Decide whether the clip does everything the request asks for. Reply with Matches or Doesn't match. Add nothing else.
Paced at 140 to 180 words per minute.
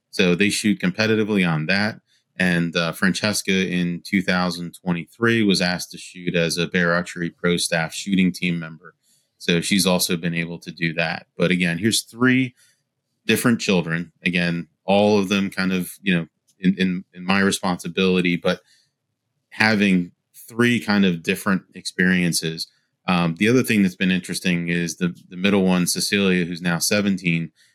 Matches